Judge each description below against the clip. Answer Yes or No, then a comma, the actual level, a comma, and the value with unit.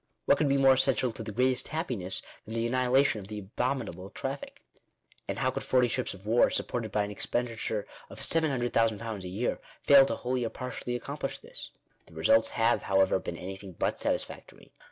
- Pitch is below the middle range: Yes, low, 115 Hz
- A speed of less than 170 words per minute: No, average, 185 wpm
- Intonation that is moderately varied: Yes, average, 3.8 semitones